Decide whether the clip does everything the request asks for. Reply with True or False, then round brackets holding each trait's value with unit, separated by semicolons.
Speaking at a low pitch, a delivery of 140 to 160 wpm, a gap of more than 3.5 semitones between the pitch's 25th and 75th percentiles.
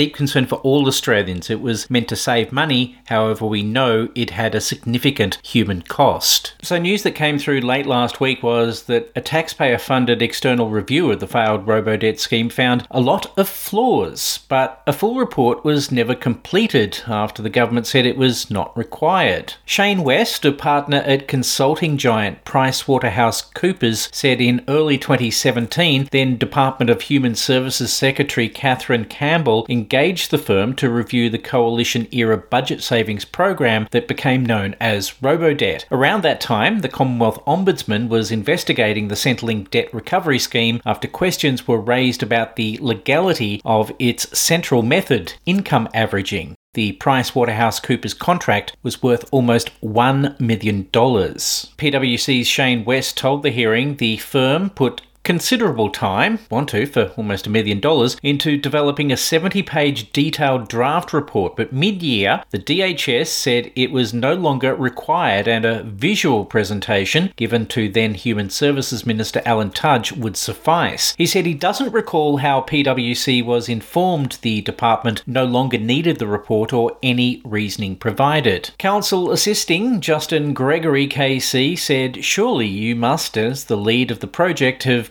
True (125 Hz; 155 wpm; 3.9 semitones)